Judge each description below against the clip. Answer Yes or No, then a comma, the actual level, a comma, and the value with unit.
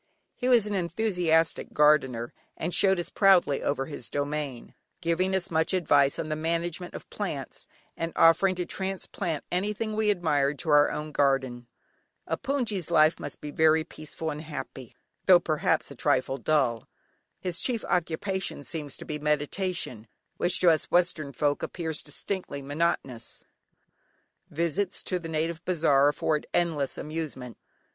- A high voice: No, medium, 160 Hz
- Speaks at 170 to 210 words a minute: No, average, 150 wpm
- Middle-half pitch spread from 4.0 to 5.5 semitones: No, average, 3.6 semitones